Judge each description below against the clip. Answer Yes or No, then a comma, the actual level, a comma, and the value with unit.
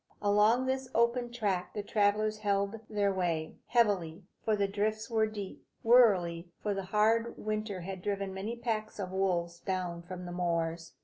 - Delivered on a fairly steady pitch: No, average, 3.1 semitones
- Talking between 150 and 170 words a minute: Yes, average, 165 wpm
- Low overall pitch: No, high, 205 Hz